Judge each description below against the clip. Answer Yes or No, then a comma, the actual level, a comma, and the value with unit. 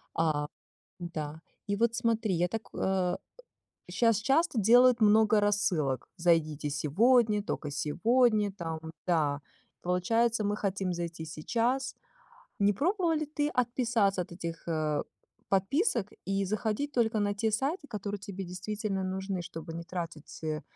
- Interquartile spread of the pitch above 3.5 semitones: Yes, average, 5.1 semitones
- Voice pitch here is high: Yes, high, 200 Hz